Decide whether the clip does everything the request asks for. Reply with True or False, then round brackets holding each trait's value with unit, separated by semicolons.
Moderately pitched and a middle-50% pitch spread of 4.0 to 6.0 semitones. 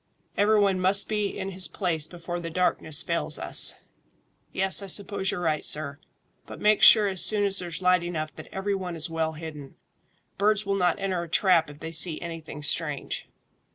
False (180 Hz; 3.4 semitones)